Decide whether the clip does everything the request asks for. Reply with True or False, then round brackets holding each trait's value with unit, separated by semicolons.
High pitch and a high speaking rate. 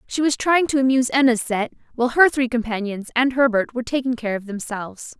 True (245 Hz; 210 wpm)